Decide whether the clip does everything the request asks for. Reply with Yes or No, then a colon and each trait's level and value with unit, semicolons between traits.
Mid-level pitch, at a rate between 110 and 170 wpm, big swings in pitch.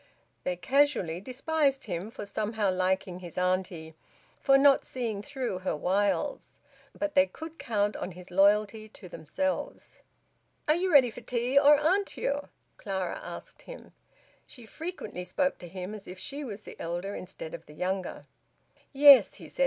No: high, 210 Hz; average, 160 wpm; wide, 7.3 semitones